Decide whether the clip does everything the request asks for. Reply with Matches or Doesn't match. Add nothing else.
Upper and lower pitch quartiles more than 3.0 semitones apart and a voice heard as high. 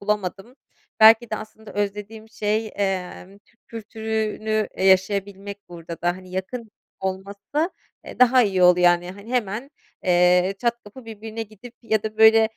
Doesn't match